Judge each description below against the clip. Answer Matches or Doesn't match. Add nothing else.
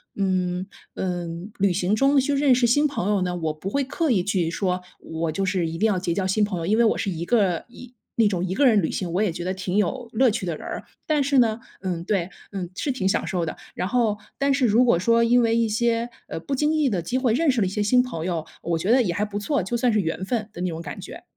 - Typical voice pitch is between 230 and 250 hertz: Doesn't match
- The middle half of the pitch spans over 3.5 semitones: Matches